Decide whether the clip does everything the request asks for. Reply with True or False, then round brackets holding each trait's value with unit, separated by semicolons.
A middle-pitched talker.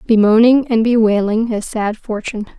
False (225 Hz)